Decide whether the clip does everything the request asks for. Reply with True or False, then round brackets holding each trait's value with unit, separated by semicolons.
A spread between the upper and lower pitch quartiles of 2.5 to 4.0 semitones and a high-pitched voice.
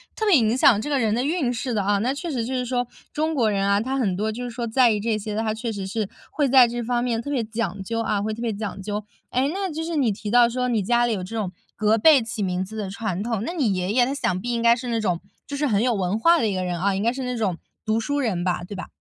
True (3.5 semitones; 230 Hz)